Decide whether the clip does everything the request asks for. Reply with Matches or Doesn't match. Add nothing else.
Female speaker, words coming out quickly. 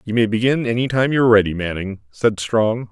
Doesn't match